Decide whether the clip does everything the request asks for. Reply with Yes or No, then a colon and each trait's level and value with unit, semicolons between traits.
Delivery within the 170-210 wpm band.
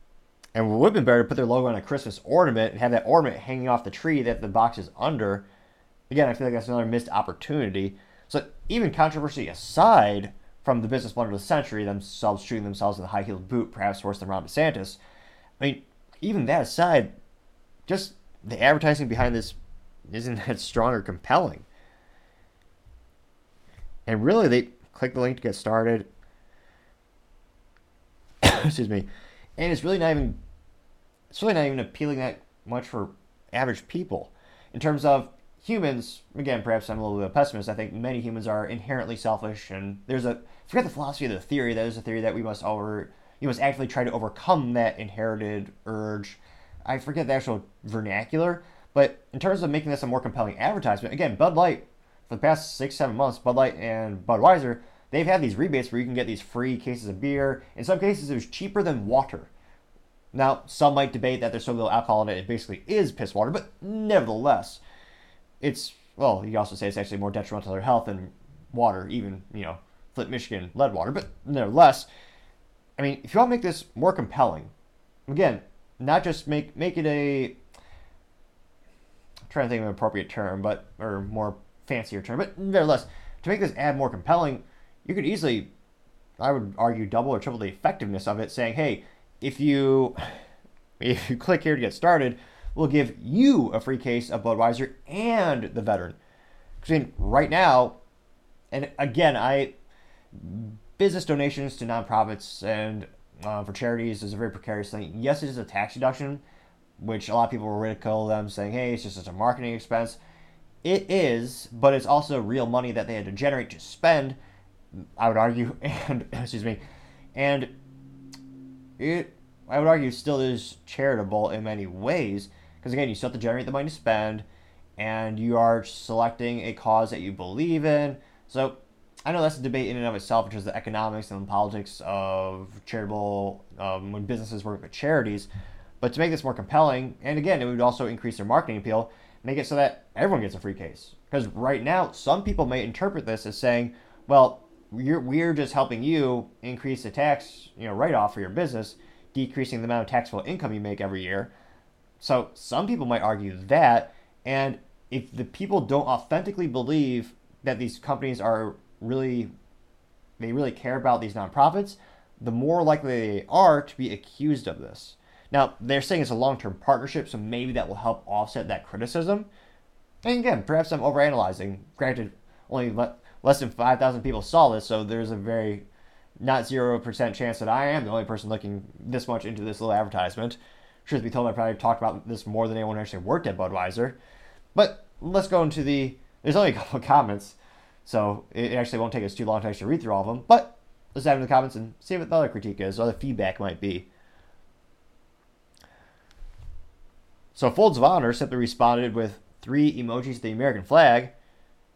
Yes: average, 190 wpm